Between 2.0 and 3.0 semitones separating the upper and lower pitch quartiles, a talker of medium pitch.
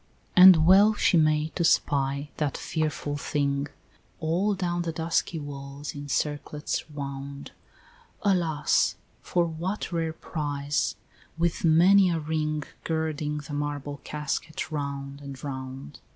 Yes: narrow, 2.6 semitones; medium, 150 Hz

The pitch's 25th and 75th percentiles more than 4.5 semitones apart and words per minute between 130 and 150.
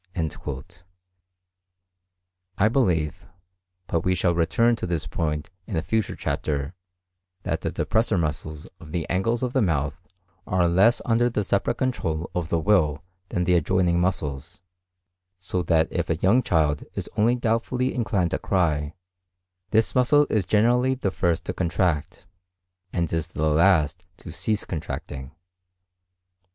Yes: average, 5.3 semitones; average, 140 wpm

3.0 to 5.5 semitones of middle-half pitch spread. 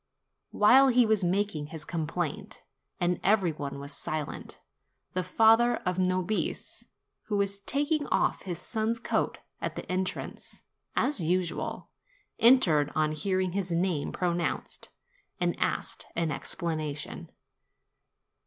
Yes: average, 4.6 semitones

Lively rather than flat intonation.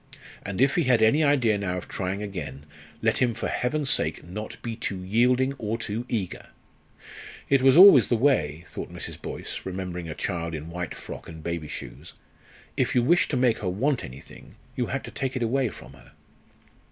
Yes: wide, 6.2 semitones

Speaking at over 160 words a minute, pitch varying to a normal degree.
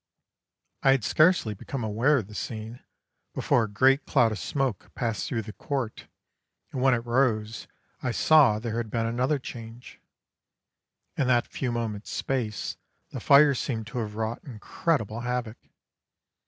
No: average, 155 wpm; average, 3.2 semitones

